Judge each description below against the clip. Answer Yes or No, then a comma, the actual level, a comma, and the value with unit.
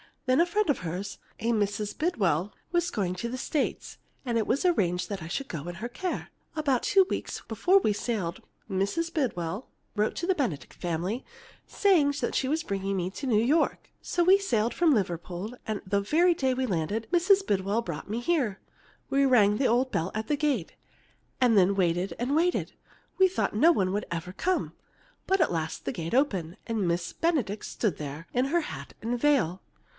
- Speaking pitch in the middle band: No, high, 225 Hz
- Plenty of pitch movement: Yes, wide, 7.9 semitones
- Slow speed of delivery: No, average, 195 wpm